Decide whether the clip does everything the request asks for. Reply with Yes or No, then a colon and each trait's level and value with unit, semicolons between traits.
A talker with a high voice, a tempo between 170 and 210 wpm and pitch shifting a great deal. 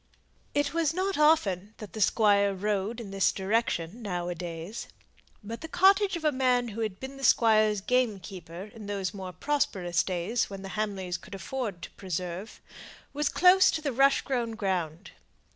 Yes: high, 210 Hz; average, 175 wpm; wide, 5.8 semitones